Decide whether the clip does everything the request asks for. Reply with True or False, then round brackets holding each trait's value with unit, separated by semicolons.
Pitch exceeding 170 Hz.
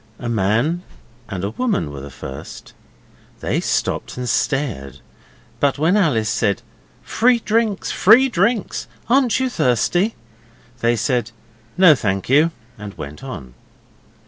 False (135 Hz)